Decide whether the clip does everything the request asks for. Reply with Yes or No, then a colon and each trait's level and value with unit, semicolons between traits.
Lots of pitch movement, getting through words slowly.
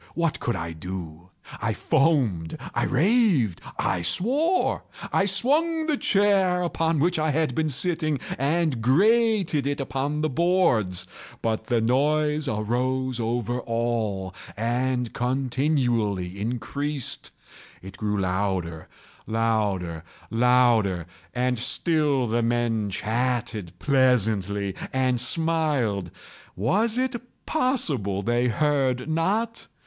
Yes: wide, 6.7 semitones; slow, 100 wpm